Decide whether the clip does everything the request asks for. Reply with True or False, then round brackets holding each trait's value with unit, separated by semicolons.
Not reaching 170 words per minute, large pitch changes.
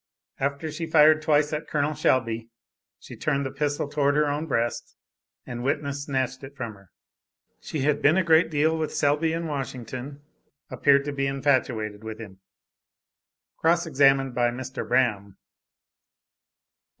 False (150 wpm; 2.9 semitones)